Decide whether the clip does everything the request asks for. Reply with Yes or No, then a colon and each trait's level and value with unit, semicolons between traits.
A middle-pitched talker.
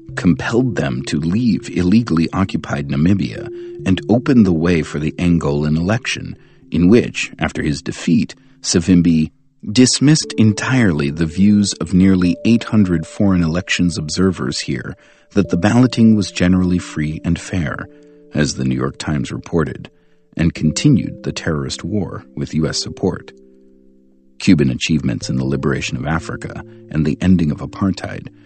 No: very low, 90 Hz